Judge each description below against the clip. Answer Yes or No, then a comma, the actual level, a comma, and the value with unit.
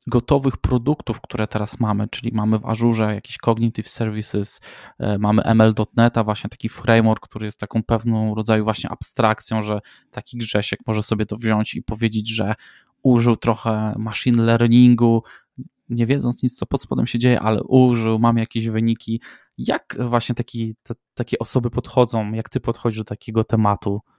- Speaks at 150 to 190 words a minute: Yes, fast, 160 wpm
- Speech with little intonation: Yes, narrow, 1.8 semitones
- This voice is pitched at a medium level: No, low, 115 Hz